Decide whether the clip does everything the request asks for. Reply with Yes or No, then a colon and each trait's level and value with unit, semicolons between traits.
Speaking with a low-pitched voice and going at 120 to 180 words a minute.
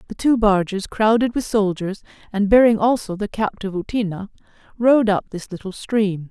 No: high, 210 Hz; average, 160 wpm